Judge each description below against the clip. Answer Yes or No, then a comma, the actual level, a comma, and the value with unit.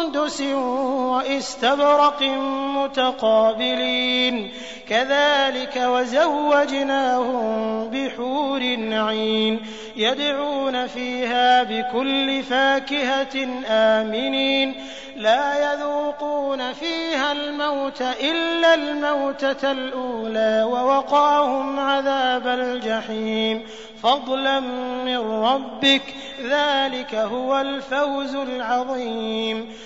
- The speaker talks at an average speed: No, slow, 55 wpm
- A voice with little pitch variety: No, average, 3.0 semitones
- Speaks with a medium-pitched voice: No, very high, 260 Hz